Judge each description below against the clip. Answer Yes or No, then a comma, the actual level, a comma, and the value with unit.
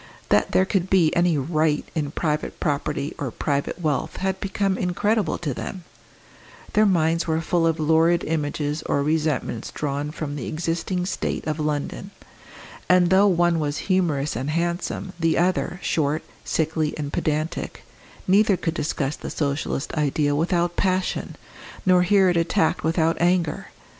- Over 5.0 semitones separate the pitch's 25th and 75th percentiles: No, average, 3.1 semitones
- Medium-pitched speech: Yes, medium, 160 Hz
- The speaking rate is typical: Yes, average, 150 wpm